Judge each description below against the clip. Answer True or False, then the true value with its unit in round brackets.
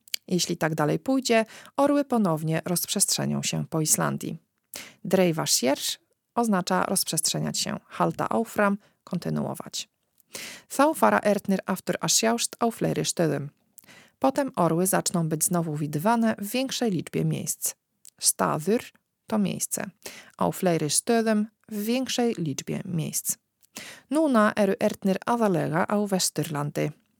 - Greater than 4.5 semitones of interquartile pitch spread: True (5.3 semitones)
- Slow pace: True (100 wpm)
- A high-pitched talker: True (195 Hz)